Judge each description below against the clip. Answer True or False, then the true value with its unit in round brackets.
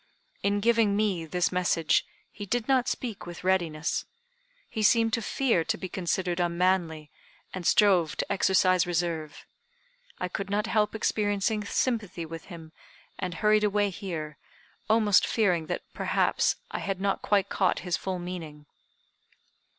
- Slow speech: False (145 wpm)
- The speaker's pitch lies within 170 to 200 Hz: True (190 Hz)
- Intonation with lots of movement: False (3.5 semitones)